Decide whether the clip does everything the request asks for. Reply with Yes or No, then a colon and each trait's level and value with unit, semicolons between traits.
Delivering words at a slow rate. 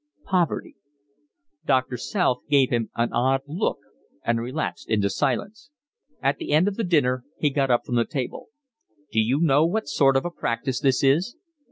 No: average, 165 wpm